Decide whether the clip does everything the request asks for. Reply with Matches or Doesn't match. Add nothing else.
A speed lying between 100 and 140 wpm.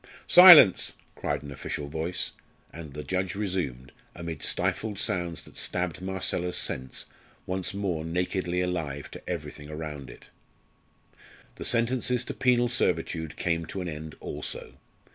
Matches